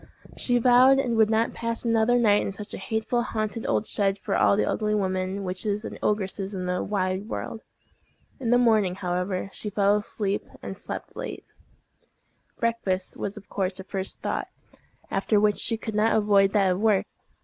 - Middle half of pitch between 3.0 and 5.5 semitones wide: No, narrow, 2.6 semitones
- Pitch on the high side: Yes, high, 210 Hz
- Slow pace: No, average, 180 wpm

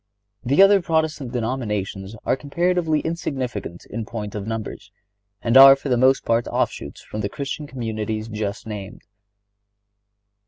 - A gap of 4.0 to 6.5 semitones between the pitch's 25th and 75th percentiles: Yes, average, 4.9 semitones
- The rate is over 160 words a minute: No, slow, 135 wpm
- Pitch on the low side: Yes, low, 120 Hz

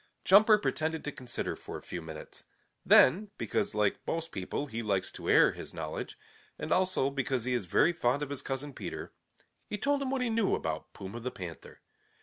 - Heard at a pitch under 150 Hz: Yes, medium, 140 Hz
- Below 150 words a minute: No, average, 195 wpm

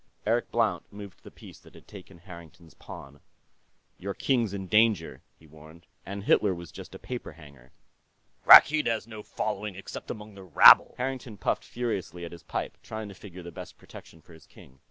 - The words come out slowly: No, average, 185 wpm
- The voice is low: Yes, very low, 95 Hz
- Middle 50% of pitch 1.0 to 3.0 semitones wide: No, average, 4.1 semitones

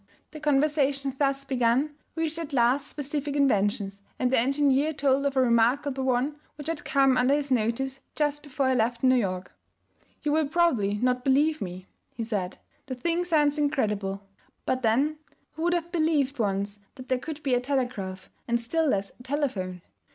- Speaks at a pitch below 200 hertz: No, very high, 270 Hz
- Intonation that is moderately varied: Yes, average, 3.9 semitones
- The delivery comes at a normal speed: Yes, average, 175 wpm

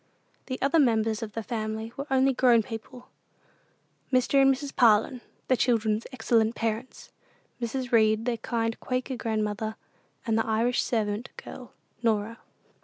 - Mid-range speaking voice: No, high, 230 Hz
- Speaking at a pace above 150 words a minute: No, average, 140 wpm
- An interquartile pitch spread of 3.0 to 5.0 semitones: No, narrow, 2.5 semitones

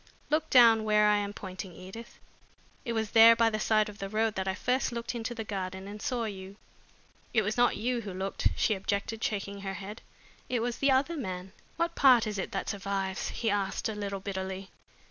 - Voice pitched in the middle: No, high, 210 Hz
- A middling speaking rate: No, fast, 210 wpm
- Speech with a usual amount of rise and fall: Yes, average, 3.0 semitones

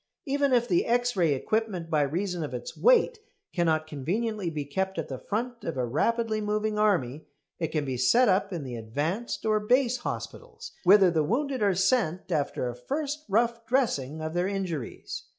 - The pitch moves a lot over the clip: Yes, wide, 7.0 semitones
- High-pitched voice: Yes, high, 195 Hz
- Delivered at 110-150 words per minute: No, average, 185 wpm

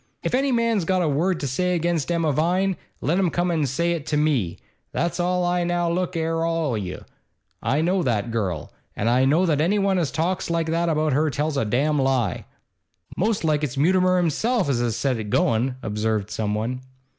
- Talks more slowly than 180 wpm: No, fast, 205 wpm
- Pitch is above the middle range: No, medium, 160 Hz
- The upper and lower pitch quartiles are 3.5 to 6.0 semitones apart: Yes, average, 5.2 semitones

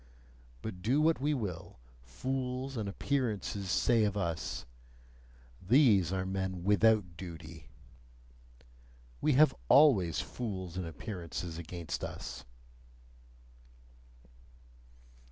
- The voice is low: Yes, very low, 95 Hz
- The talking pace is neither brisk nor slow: No, slow, 95 wpm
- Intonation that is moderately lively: No, wide, 6.4 semitones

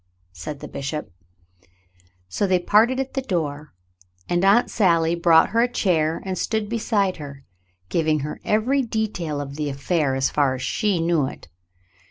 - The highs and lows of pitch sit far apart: Yes, wide, 6.3 semitones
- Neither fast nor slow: Yes, average, 170 wpm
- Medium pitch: Yes, medium, 170 Hz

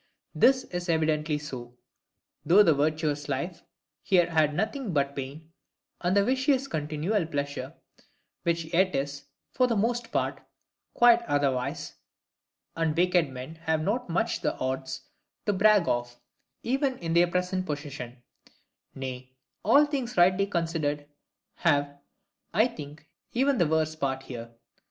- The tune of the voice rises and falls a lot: Yes, wide, 5.8 semitones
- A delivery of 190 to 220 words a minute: No, slow, 135 wpm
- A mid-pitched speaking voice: Yes, medium, 160 Hz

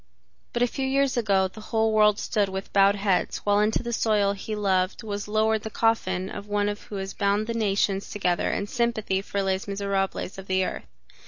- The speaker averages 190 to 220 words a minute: Yes, average, 200 wpm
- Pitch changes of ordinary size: No, narrow, 2.0 semitones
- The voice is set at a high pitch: Yes, high, 205 Hz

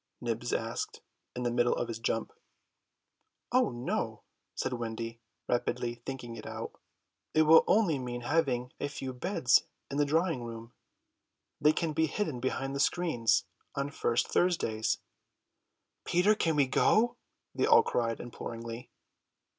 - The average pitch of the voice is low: Yes, low, 125 Hz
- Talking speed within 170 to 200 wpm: No, average, 140 wpm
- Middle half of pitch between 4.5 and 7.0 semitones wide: Yes, average, 4.9 semitones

